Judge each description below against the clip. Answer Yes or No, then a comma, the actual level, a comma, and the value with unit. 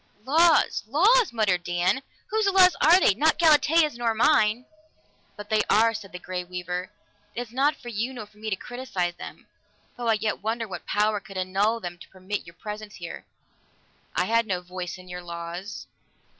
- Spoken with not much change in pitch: No, average, 5.0 semitones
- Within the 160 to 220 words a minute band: Yes, average, 185 wpm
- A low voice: No, high, 215 Hz